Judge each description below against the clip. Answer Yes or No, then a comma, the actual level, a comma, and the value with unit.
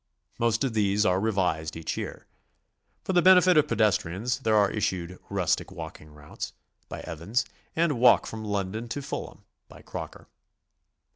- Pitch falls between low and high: No, low, 105 Hz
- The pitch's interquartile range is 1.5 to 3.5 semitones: No, average, 4.8 semitones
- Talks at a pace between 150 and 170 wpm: Yes, average, 155 wpm